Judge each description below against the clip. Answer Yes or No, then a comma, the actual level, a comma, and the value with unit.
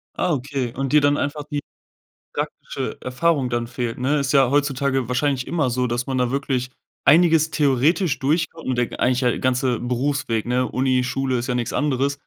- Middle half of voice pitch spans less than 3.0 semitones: Yes, narrow, 2.5 semitones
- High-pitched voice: No, low, 135 Hz